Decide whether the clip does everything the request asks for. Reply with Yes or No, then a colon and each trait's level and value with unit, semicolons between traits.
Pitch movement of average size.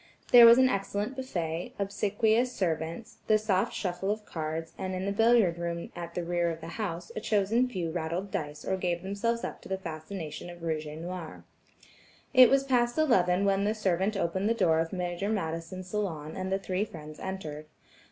Yes: average, 3.9 semitones